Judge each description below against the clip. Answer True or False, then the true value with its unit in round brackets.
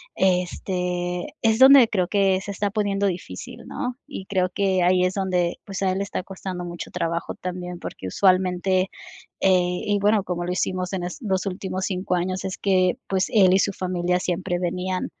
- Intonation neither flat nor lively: False (1.5 semitones)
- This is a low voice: False (185 Hz)